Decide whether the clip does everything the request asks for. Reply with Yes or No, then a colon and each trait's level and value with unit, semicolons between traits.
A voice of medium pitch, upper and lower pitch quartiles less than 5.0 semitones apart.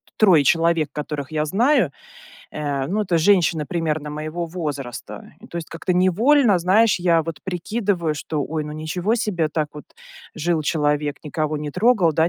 Yes: medium, 165 Hz; average, 3.3 semitones